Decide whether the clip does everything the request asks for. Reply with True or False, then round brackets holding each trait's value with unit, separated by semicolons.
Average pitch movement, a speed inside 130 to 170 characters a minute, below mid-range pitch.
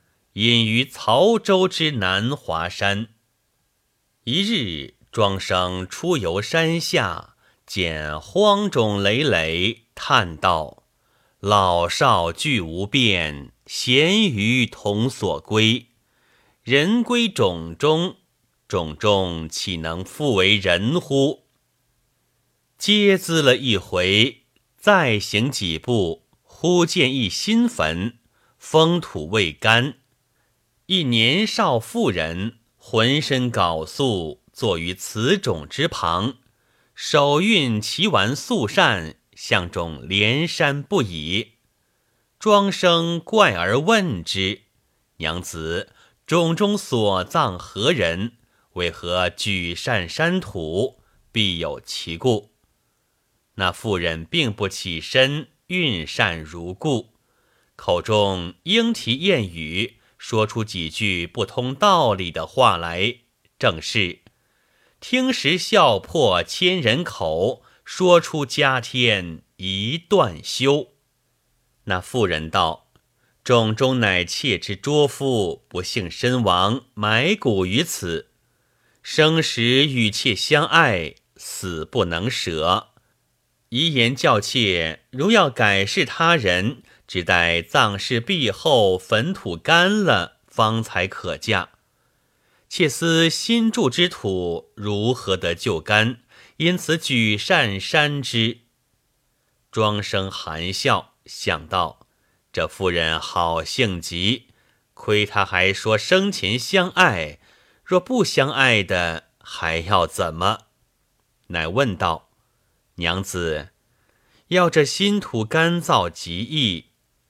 False (7.9 semitones; 140 characters per minute; 115 Hz)